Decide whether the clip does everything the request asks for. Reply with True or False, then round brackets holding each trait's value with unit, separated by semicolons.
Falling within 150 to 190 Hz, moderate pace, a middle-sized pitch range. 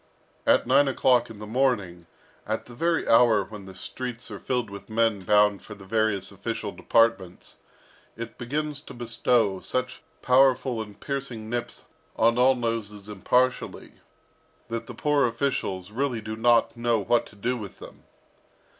False (115 Hz; 155 wpm; 3.2 semitones)